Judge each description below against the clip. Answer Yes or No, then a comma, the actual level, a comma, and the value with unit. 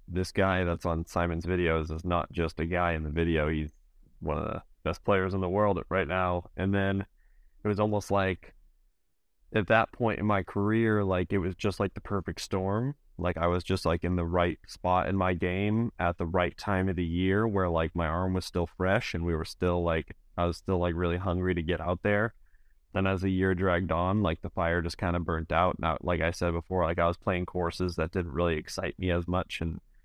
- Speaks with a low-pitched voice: Yes, very low, 90 Hz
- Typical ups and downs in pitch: No, narrow, 2.1 semitones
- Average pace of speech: No, fast, 240 wpm